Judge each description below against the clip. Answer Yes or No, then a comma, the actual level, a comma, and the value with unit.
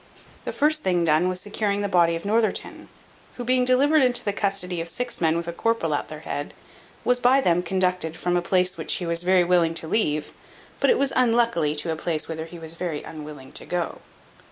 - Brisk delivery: Yes, fast, 220 wpm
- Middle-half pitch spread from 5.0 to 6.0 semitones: Yes, wide, 5.6 semitones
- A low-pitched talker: No, medium, 180 Hz